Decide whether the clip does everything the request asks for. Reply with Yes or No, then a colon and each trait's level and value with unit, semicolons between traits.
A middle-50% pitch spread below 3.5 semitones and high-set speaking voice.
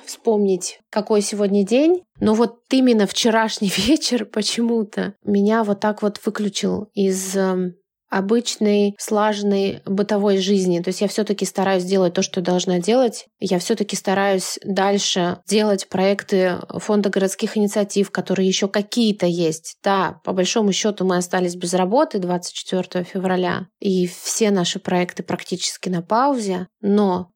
Yes: narrow, 2.4 semitones; high, 200 Hz